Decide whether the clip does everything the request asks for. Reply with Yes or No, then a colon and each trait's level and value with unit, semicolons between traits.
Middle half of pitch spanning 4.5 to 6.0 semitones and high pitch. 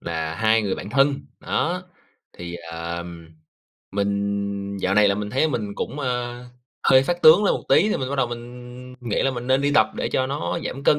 No: average, 5.0 semitones; low, 120 Hz